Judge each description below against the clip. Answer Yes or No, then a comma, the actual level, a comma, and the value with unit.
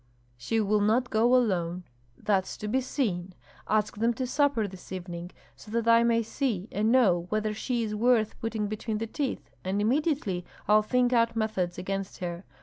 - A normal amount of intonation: Yes, average, 3.5 semitones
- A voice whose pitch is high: Yes, high, 215 Hz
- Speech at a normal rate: Yes, average, 180 wpm